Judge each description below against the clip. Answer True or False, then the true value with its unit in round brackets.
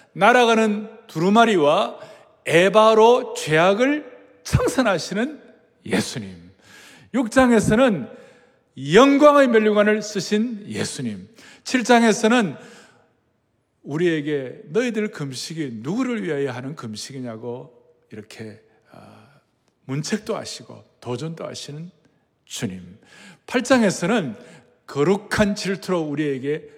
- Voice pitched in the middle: False (195 Hz)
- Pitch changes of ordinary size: False (8.4 semitones)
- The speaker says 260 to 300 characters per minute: False (215 characters per minute)